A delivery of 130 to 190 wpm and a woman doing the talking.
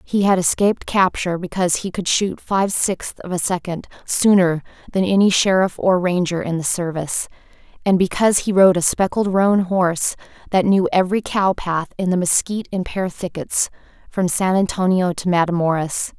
Yes: average, 170 wpm; female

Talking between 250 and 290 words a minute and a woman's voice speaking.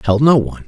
No: fast, 265 wpm; male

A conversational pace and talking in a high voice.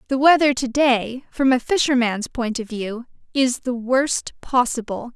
Yes: average, 165 wpm; very high, 250 Hz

